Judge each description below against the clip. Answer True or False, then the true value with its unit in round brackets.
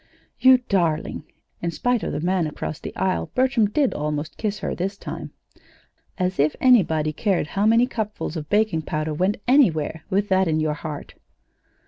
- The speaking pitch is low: False (185 Hz)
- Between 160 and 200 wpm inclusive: True (170 wpm)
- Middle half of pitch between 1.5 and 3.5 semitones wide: False (5.5 semitones)